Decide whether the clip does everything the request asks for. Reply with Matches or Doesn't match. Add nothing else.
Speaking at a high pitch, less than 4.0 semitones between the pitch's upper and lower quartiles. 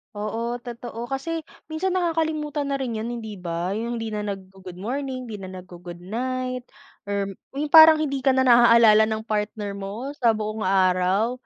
Doesn't match